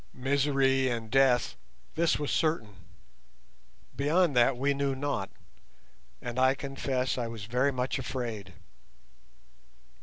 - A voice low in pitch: Yes, low, 130 Hz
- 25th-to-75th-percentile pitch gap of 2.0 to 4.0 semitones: Yes, narrow, 2.6 semitones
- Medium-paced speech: No, slow, 115 wpm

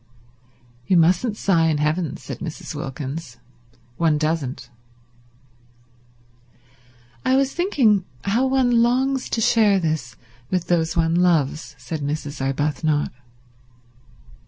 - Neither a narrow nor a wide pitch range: No, wide, 6.2 semitones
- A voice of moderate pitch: Yes, medium, 165 Hz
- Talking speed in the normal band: No, slow, 110 wpm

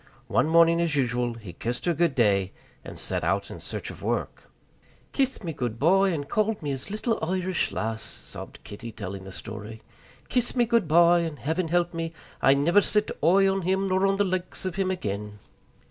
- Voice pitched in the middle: Yes, medium, 165 Hz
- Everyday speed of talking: Yes, average, 190 wpm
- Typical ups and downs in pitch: No, wide, 7.6 semitones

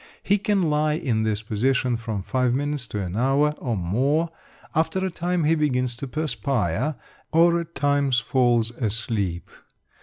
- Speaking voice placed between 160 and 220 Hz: No, low, 130 Hz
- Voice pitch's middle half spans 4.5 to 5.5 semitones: Yes, average, 5.2 semitones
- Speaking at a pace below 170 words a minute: Yes, average, 155 wpm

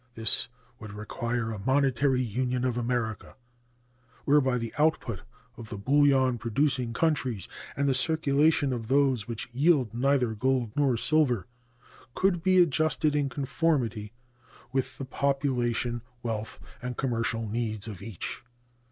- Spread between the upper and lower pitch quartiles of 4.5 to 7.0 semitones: No, average, 3.6 semitones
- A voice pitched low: Yes, low, 125 Hz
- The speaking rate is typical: No, slow, 130 wpm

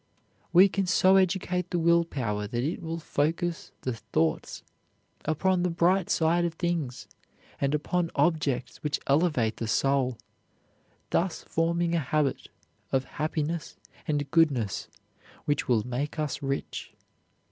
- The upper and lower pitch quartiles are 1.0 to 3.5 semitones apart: No, average, 4.0 semitones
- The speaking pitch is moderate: Yes, medium, 155 Hz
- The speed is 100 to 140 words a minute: Yes, slow, 135 wpm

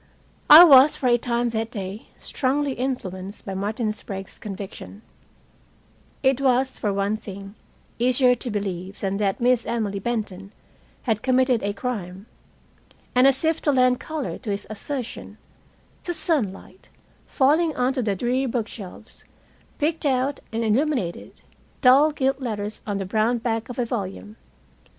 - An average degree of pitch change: Yes, average, 4.5 semitones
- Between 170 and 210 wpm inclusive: No, average, 140 wpm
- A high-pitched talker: Yes, high, 235 Hz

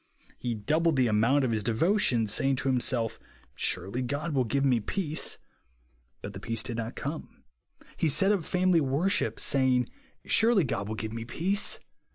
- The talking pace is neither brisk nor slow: Yes, average, 170 wpm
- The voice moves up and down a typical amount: No, wide, 6.0 semitones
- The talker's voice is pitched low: Yes, low, 130 Hz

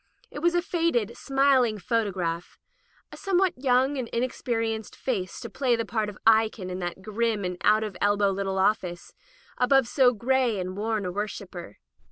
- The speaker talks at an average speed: Yes, average, 180 wpm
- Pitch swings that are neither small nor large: Yes, average, 4.5 semitones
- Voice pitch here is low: No, high, 220 Hz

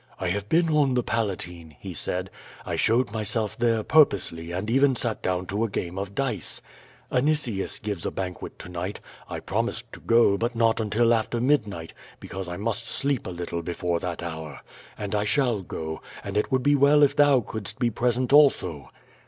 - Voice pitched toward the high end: No, low, 110 Hz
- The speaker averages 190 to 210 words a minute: Yes, average, 195 wpm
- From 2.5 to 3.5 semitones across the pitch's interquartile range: No, average, 5.3 semitones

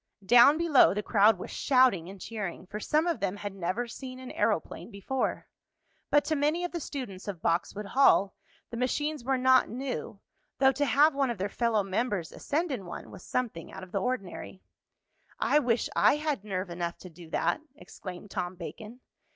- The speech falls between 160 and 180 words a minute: No, average, 190 wpm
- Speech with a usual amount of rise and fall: No, wide, 5.9 semitones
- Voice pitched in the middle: No, high, 230 Hz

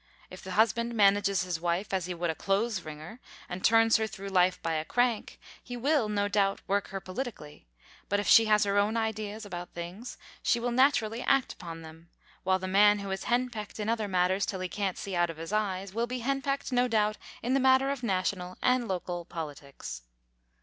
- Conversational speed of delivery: No, fast, 210 wpm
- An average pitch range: Yes, average, 4.1 semitones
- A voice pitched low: No, high, 205 Hz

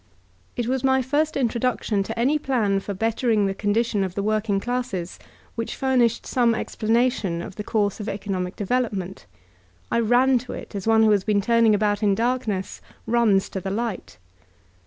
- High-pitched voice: Yes, high, 220 Hz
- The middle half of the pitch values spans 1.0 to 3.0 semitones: No, average, 3.4 semitones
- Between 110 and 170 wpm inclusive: No, average, 185 wpm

